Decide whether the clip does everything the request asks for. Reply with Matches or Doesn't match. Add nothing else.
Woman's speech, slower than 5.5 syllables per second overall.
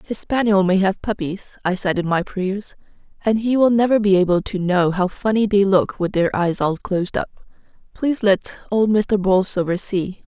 Matches